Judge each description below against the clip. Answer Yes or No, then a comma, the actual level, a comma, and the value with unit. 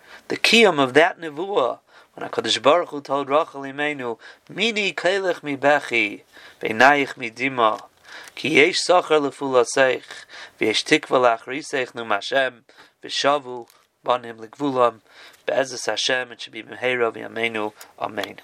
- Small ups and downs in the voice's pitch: No, average, 3.7 semitones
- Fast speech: No, average, 135 wpm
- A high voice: No, low, 135 Hz